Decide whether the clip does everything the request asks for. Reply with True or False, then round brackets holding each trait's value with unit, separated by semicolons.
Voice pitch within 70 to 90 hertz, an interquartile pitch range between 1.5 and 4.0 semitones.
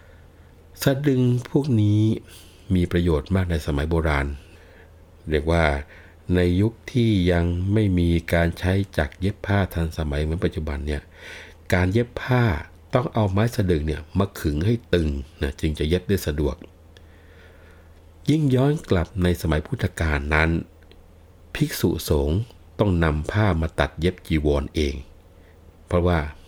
True (85 Hz; 3.3 semitones)